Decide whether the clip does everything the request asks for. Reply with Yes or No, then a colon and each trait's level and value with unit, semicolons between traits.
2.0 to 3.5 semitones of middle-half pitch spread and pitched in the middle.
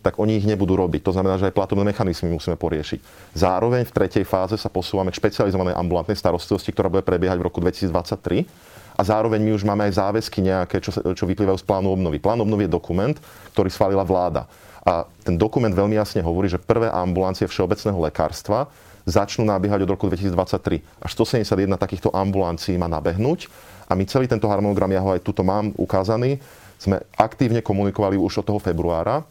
No: narrow, 2.6 semitones; very low, 95 Hz